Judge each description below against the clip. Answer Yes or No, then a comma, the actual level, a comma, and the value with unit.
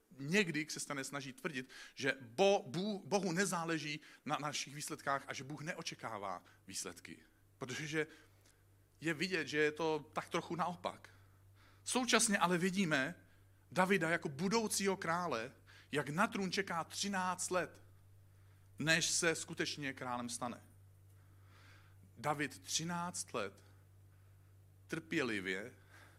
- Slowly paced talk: Yes, slow, 110 wpm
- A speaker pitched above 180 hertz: No, low, 135 Hz